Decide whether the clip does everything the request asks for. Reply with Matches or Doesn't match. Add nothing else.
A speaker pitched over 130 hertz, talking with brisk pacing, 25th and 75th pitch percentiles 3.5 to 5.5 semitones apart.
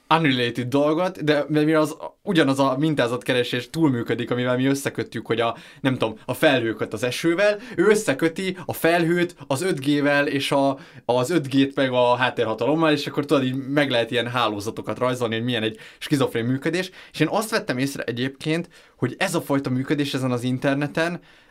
Matches